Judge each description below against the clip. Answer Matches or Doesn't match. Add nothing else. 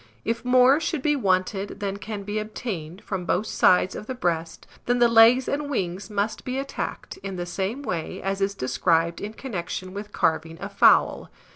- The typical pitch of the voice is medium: Doesn't match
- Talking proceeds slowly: Doesn't match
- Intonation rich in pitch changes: Doesn't match